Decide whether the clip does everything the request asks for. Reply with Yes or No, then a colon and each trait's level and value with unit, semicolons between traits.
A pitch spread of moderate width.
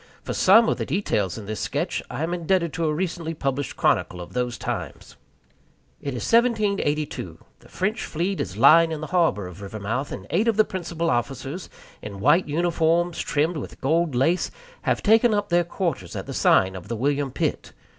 No: wide, 6.0 semitones